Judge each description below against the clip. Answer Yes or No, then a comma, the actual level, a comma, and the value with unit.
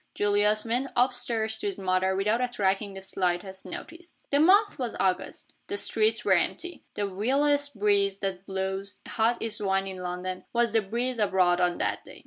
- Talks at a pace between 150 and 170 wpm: No, average, 185 wpm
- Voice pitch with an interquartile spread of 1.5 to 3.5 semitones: No, average, 4.1 semitones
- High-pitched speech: Yes, high, 205 Hz